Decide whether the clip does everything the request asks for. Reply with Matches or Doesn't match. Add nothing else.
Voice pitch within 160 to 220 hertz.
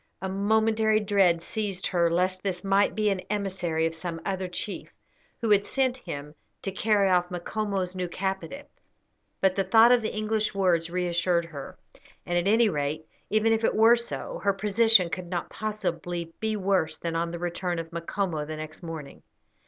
Matches